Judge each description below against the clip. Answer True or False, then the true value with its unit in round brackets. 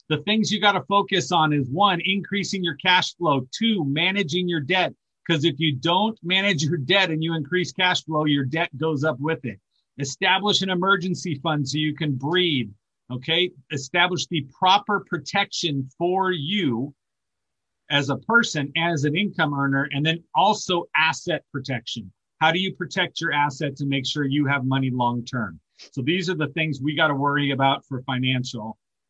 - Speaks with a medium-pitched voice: True (160 Hz)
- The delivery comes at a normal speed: True (180 wpm)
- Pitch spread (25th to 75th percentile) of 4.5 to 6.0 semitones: True (4.8 semitones)